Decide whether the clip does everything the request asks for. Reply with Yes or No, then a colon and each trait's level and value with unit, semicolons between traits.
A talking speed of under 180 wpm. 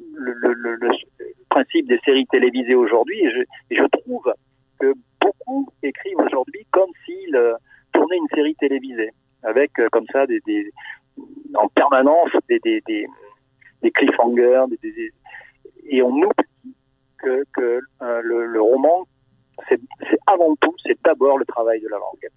Yes: average, 160 wpm